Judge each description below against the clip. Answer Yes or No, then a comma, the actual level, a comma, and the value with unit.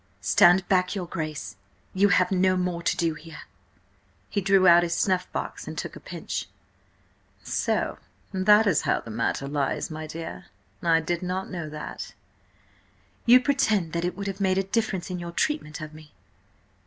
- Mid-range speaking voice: Yes, medium, 180 Hz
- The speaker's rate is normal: Yes, average, 175 wpm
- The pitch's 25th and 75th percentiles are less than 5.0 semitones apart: Yes, average, 3.0 semitones